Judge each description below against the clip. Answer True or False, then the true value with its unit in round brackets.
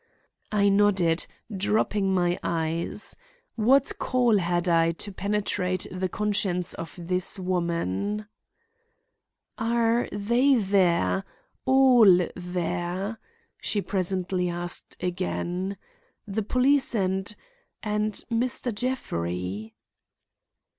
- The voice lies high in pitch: True (195 Hz)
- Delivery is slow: True (85 wpm)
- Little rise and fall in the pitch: False (3.5 semitones)